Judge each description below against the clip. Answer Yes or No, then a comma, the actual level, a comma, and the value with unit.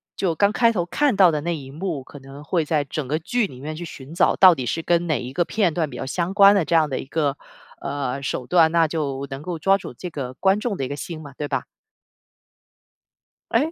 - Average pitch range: Yes, average, 4.4 semitones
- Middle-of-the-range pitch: Yes, medium, 160 Hz